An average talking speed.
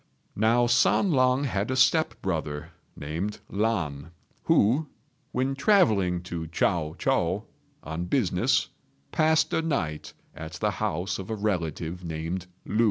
No: slow, 130 wpm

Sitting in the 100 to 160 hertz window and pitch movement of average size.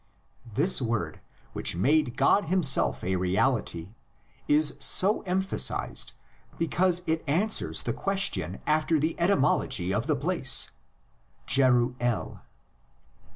No: medium, 140 Hz; wide, 7.1 semitones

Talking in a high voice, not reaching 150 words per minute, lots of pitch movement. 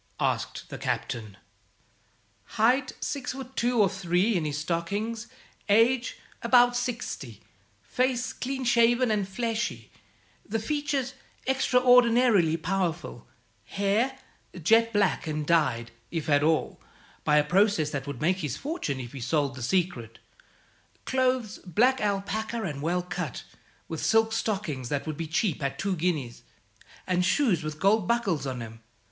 Yes: high, 195 Hz; average, 140 wpm; wide, 7.5 semitones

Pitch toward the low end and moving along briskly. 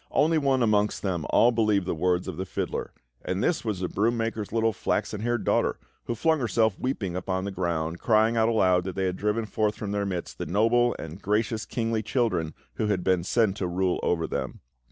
Yes: low, 105 Hz; fast, 215 wpm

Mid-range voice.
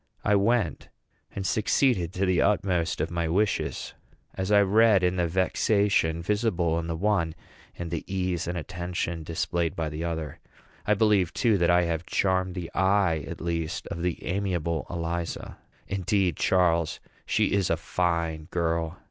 No: very low, 90 Hz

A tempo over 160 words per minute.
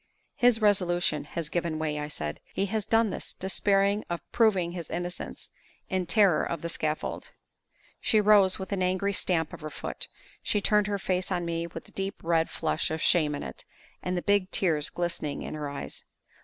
Yes: average, 195 wpm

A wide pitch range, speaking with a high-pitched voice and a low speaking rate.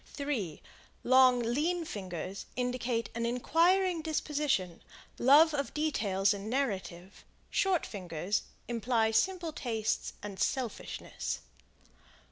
Yes: wide, 6.8 semitones; high, 245 Hz; slow, 95 wpm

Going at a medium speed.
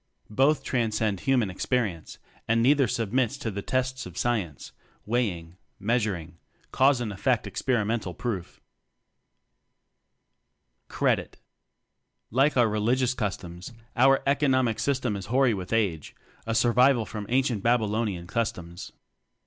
No: slow, 130 wpm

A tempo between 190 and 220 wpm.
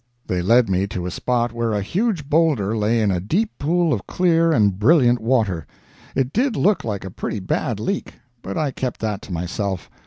Yes: fast, 205 wpm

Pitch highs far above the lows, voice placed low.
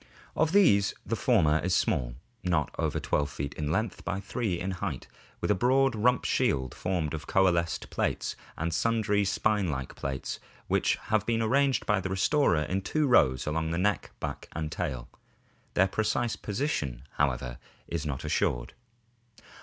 Yes: wide, 6.4 semitones; very low, 90 Hz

